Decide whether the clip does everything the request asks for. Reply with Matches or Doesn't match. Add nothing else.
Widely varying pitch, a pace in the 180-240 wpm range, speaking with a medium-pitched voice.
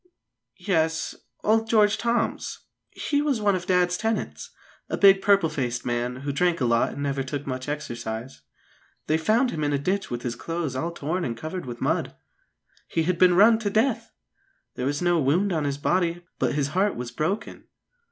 Matches